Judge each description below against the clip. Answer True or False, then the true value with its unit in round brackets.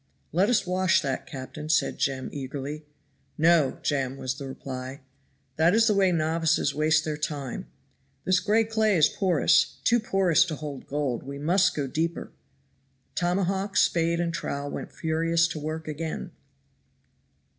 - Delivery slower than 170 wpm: True (150 wpm)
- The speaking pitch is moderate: True (160 Hz)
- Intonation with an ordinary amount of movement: True (3.9 semitones)